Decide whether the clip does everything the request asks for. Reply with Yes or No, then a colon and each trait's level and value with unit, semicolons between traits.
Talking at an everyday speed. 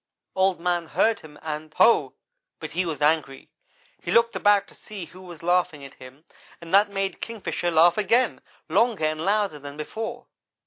Yes: average, 175 wpm